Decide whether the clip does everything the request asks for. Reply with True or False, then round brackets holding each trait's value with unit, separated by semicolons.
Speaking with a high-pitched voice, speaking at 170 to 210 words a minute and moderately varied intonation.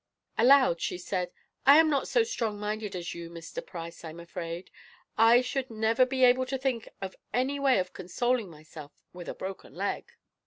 False (220 Hz; 185 wpm; 6.6 semitones)